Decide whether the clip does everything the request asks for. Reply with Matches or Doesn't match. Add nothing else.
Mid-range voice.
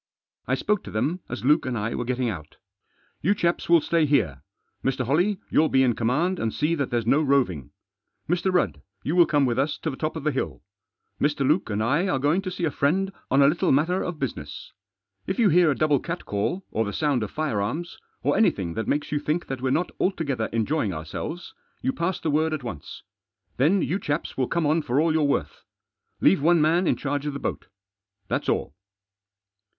Matches